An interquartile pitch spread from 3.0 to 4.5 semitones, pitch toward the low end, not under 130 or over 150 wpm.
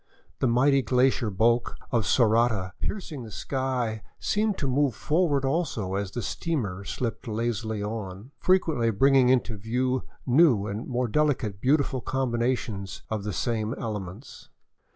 Yes: average, 3.8 semitones; low, 120 Hz; average, 140 wpm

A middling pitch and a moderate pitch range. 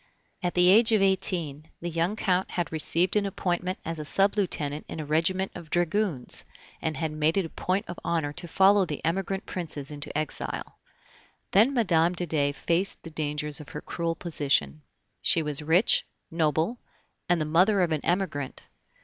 Yes: medium, 170 Hz; average, 3.5 semitones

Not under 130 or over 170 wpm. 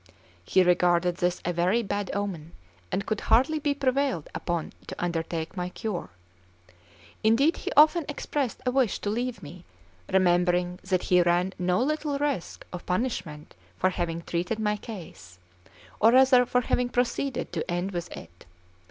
Yes: average, 160 wpm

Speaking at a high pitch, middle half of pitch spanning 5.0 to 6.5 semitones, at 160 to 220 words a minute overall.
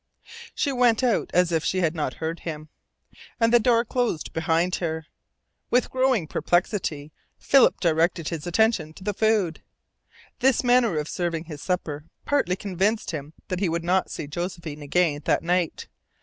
No: medium, 175 Hz; wide, 5.5 semitones; average, 165 wpm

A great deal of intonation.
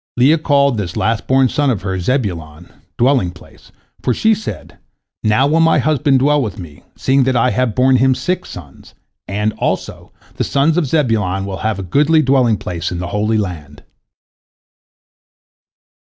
Yes: wide, 6.3 semitones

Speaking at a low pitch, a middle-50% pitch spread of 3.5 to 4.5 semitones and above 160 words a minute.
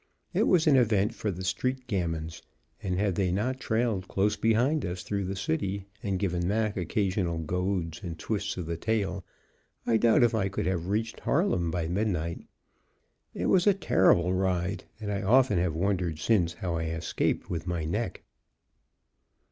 Yes: very low, 95 Hz; average, 3.9 semitones; average, 170 wpm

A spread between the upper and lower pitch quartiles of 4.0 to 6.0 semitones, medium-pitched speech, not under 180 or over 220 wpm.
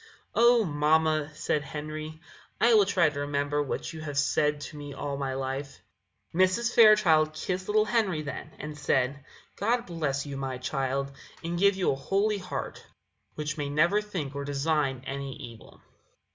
No: average, 4.6 semitones; medium, 150 Hz; average, 165 wpm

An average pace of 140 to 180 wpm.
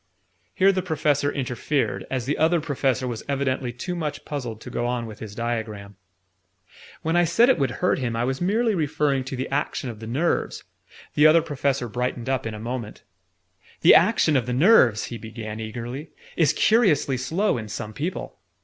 No: average, 190 wpm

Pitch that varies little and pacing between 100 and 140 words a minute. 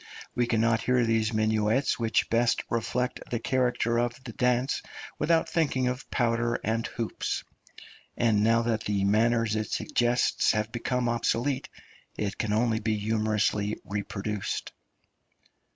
Yes: narrow, 2.0 semitones; slow, 135 wpm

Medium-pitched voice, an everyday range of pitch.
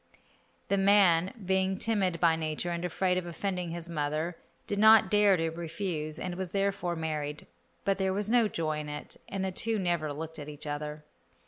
Yes: medium, 175 Hz; average, 3.6 semitones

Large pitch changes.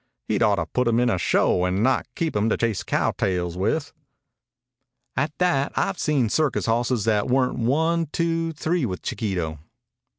Yes: wide, 7.0 semitones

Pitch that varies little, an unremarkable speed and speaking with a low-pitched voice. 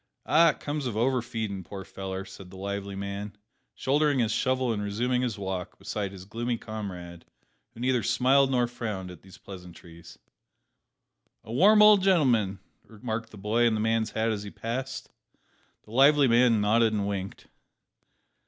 No: average, 4.1 semitones; average, 170 wpm; low, 110 Hz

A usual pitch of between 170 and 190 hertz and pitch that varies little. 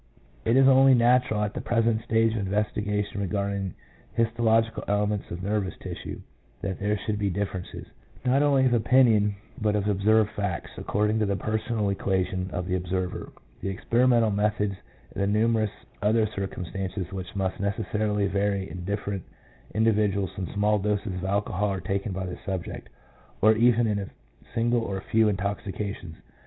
No: low, 105 Hz; narrow, 2.2 semitones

